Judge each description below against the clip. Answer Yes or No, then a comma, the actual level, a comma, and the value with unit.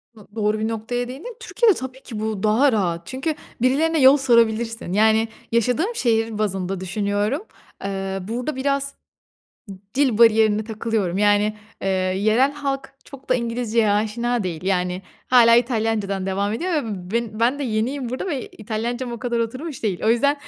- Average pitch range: Yes, average, 3.5 semitones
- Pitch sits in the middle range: No, high, 230 Hz